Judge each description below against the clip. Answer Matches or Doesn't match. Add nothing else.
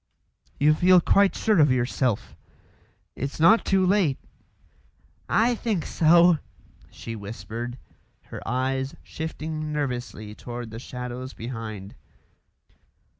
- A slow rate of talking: Matches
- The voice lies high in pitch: Doesn't match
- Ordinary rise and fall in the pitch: Doesn't match